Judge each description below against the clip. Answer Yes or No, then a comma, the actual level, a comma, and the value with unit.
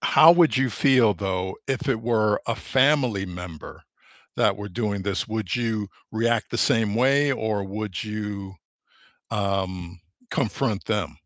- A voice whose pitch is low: Yes, low, 110 Hz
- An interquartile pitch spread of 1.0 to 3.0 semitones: No, average, 3.4 semitones